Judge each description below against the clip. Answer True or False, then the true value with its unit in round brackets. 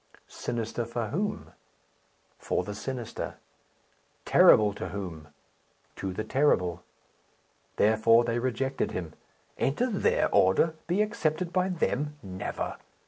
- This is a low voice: True (120 Hz)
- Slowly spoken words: True (110 wpm)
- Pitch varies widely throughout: True (7.3 semitones)